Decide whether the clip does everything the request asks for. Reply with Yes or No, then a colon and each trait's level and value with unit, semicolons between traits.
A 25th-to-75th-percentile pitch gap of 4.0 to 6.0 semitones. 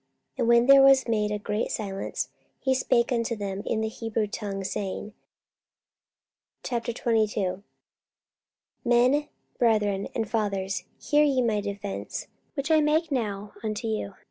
No: average, 3.2 semitones